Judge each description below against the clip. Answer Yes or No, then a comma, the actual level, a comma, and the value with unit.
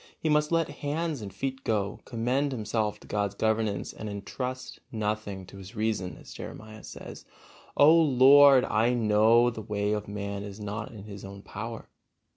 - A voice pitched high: No, low, 110 Hz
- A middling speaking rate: Yes, average, 175 wpm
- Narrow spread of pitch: No, average, 4.0 semitones